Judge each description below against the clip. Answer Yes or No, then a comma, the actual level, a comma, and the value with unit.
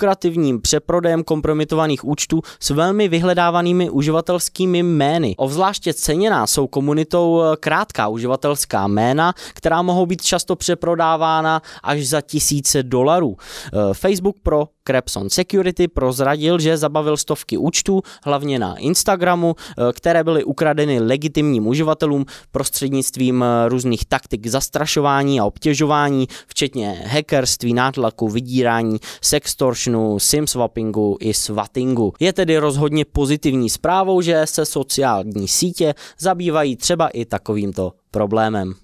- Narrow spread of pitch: No, average, 4.9 semitones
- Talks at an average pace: No, slow, 105 wpm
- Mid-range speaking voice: Yes, medium, 150 Hz